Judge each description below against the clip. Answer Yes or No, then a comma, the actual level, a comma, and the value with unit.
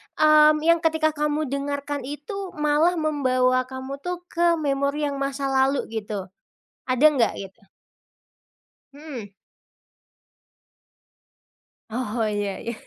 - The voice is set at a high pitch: Yes, very high, 280 Hz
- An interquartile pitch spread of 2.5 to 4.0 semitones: Yes, average, 3.3 semitones